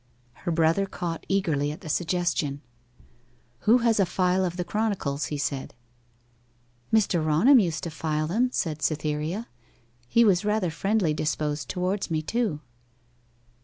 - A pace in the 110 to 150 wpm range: Yes, average, 140 wpm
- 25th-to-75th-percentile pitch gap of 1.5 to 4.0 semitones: No, average, 4.4 semitones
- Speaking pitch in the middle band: Yes, medium, 170 Hz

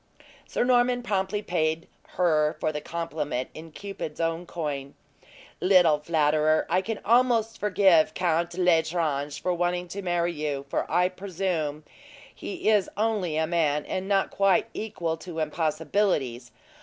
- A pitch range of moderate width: Yes, average, 3.7 semitones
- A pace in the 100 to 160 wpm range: Yes, average, 140 wpm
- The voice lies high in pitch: No, medium, 170 Hz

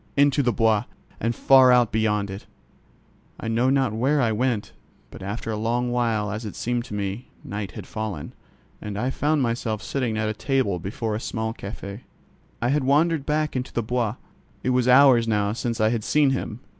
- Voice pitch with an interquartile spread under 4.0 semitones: Yes, average, 3.3 semitones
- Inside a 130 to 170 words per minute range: No, average, 195 wpm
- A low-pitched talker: Yes, low, 115 Hz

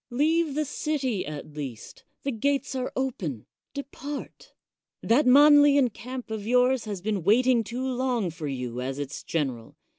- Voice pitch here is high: Yes, high, 245 Hz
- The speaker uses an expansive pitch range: Yes, wide, 8.7 semitones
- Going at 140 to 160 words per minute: Yes, average, 150 wpm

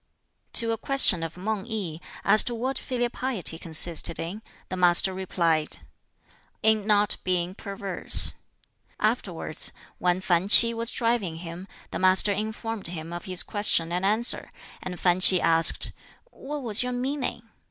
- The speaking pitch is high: Yes, high, 195 Hz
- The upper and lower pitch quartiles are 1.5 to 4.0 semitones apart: No, average, 4.5 semitones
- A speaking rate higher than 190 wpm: No, average, 150 wpm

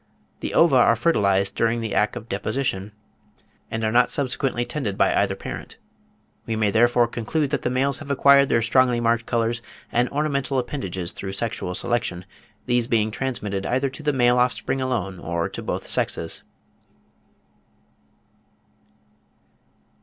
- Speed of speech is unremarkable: Yes, average, 145 wpm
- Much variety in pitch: No, average, 3.7 semitones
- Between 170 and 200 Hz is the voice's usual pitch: No, low, 120 Hz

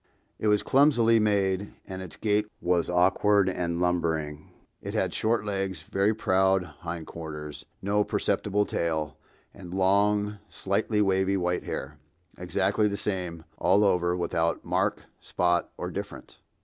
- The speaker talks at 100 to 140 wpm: Yes, slow, 135 wpm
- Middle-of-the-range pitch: No, very low, 95 Hz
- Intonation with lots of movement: No, average, 3.0 semitones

